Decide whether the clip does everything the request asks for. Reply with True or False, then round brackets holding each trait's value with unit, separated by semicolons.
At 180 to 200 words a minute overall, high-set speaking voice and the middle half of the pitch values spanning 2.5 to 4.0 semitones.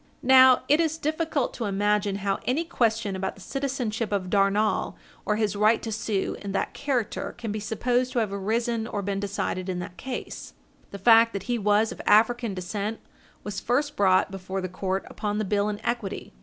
True (195 wpm; 210 Hz; 3.4 semitones)